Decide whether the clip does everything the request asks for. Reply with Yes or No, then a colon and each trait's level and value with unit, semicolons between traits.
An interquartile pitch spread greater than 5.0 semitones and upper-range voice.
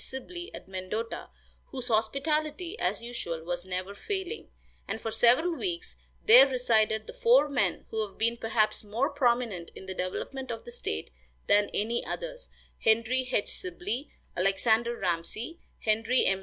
Yes: wide, 5.4 semitones; high, 235 Hz